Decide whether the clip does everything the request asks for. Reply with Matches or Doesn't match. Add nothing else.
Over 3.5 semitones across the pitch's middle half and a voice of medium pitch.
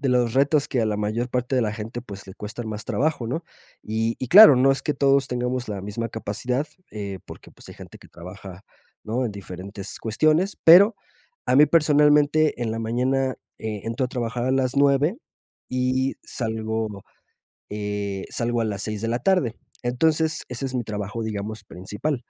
Doesn't match